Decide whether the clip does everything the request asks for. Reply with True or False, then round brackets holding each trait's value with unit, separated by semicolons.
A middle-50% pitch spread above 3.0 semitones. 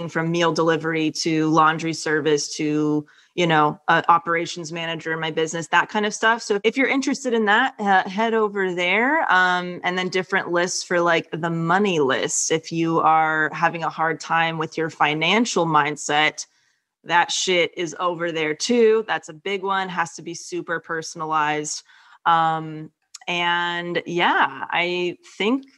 False (2.6 semitones)